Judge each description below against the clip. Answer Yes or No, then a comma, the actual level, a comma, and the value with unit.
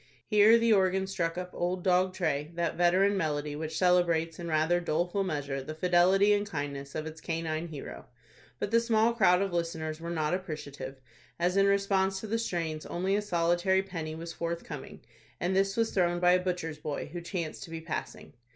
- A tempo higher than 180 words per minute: Yes, average, 190 wpm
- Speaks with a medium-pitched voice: Yes, medium, 175 Hz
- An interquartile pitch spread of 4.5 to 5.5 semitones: No, average, 3.2 semitones